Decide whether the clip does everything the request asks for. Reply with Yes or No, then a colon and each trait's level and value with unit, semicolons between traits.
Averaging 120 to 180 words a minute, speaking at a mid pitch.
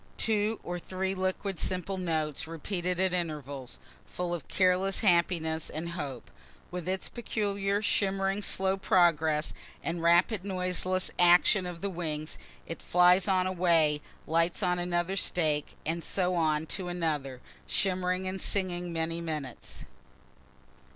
Yes: slow, 135 wpm; medium, 180 Hz